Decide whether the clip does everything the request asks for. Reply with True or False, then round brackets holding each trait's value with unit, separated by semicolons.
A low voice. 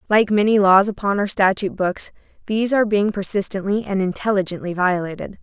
False (200 Hz)